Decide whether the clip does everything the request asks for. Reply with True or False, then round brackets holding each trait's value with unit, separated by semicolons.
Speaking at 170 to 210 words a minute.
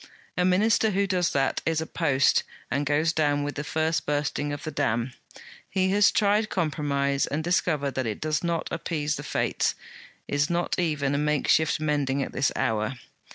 True (180 wpm)